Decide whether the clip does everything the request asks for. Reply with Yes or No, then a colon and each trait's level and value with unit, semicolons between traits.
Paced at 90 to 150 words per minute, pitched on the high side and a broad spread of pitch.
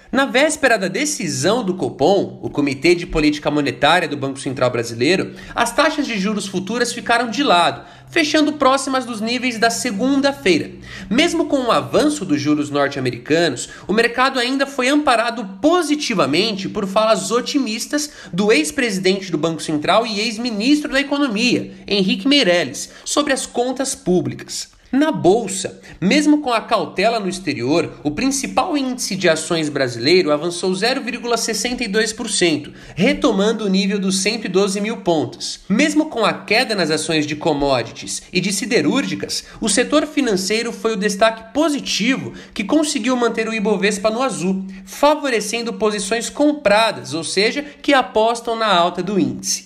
Yes: average, 145 wpm; high, 225 Hz; wide, 6.6 semitones